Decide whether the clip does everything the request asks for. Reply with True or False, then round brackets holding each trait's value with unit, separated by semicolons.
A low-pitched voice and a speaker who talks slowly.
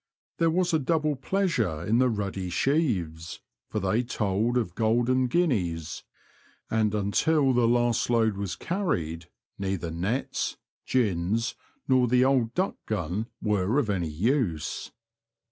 True (115 Hz; 130 wpm)